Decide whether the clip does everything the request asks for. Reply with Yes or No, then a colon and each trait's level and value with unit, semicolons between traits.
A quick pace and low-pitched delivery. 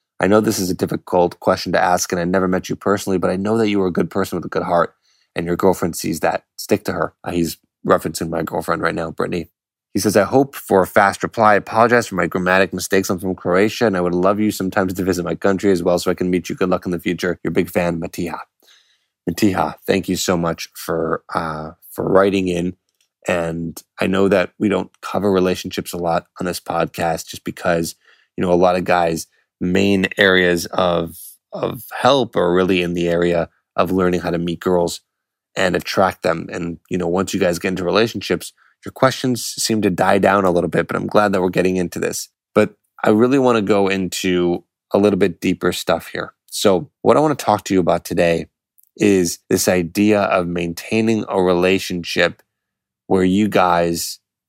Yes: fast, 215 wpm; very low, 90 Hz